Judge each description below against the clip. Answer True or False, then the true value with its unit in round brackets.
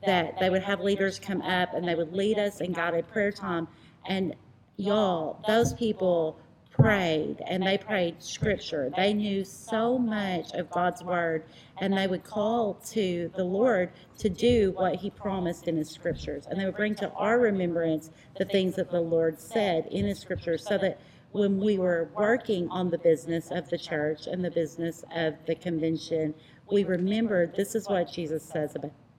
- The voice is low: False (180 Hz)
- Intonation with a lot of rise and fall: False (3.2 semitones)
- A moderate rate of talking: True (185 wpm)